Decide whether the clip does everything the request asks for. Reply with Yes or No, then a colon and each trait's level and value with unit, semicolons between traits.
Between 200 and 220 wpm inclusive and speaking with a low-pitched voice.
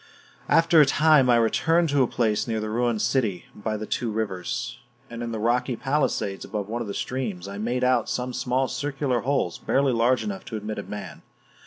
Yes: fast, 205 wpm; low, 120 Hz